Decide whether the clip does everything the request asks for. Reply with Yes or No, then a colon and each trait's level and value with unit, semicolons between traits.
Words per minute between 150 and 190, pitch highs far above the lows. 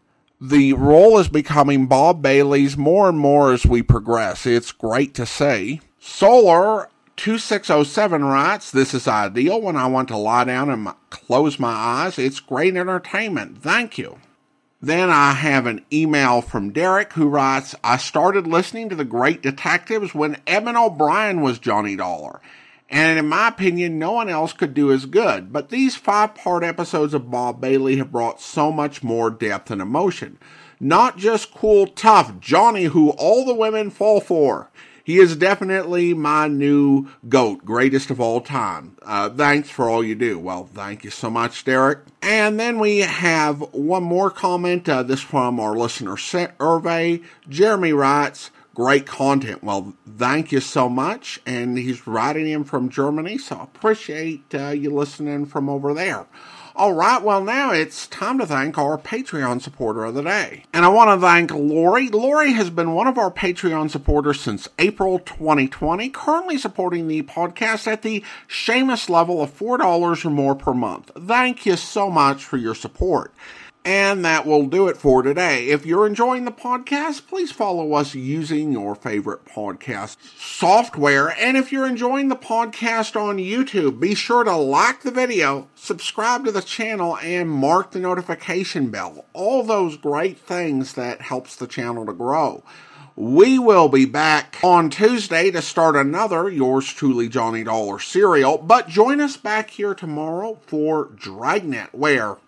Yes: average, 165 wpm; wide, 6.6 semitones